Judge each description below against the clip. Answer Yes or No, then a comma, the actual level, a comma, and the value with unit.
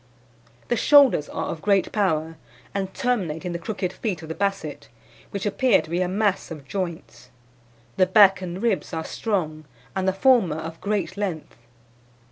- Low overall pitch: No, medium, 185 Hz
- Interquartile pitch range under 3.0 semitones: No, average, 4.0 semitones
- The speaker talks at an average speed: Yes, average, 170 wpm